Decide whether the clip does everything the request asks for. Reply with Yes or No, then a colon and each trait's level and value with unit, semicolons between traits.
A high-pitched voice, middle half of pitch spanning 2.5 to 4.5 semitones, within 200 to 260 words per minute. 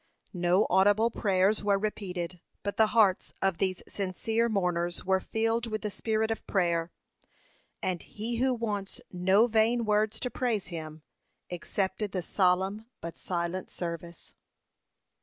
No: high, 195 Hz; average, 3.4 semitones; average, 140 wpm